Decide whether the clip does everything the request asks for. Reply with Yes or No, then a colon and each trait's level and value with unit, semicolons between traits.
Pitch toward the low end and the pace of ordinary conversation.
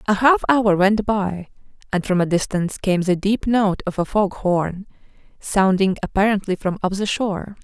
No: high, 195 Hz; average, 180 wpm